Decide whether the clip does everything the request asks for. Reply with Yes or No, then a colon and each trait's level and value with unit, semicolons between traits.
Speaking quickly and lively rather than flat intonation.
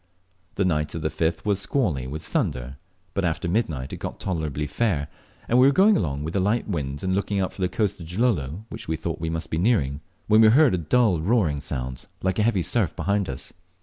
Yes: fast, 230 wpm; wide, 5.7 semitones